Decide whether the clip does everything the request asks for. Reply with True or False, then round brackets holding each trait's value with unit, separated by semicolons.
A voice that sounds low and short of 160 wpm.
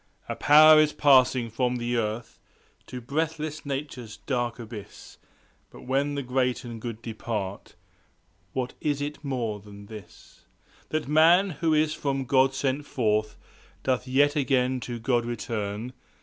True (125 Hz; 150 wpm)